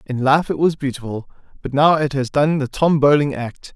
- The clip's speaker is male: Yes, male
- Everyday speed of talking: No, fast, 225 wpm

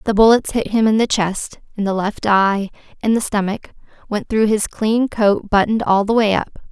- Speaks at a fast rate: Yes, fast, 215 wpm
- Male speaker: No, female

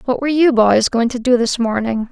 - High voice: Yes, high, 245 Hz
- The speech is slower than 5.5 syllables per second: No, 5.6 syllables/s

